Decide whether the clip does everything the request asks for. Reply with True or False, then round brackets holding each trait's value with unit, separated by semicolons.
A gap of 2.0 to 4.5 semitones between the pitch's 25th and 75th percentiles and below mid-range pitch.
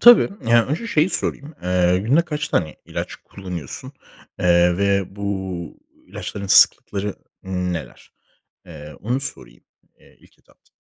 False (5.5 semitones; 95 Hz)